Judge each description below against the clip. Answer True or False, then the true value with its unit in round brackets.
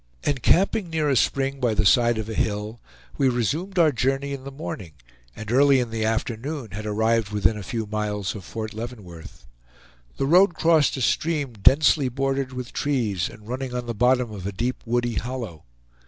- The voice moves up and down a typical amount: True (4.1 semitones)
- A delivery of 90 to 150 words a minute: False (185 wpm)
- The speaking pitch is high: False (120 Hz)